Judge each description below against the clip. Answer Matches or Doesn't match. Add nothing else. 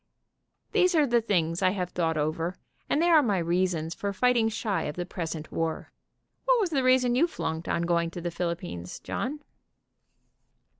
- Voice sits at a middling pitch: Matches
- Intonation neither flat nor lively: Doesn't match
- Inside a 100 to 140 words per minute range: Doesn't match